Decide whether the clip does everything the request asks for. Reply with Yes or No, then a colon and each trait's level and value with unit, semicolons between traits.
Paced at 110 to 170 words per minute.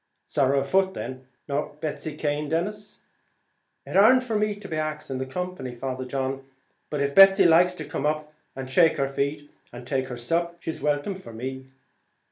No: average, 180 wpm